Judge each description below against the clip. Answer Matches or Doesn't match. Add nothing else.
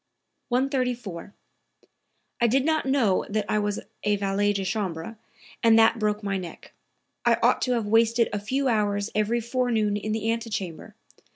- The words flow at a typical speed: Matches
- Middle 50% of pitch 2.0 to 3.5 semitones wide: Matches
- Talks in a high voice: Matches